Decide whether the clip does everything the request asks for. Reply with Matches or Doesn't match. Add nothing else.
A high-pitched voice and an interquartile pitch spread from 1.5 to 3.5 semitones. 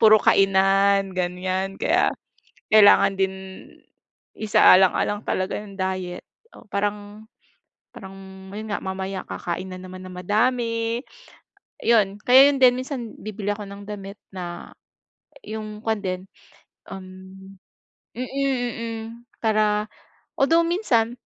Matches